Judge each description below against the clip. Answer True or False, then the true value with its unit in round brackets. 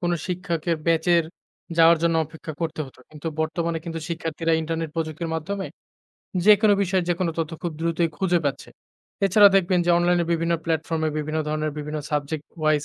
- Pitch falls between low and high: True (165 Hz)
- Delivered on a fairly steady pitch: True (1.7 semitones)